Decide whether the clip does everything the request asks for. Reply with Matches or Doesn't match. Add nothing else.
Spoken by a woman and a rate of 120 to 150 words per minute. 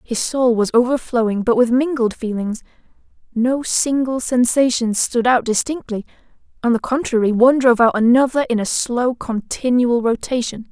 Matches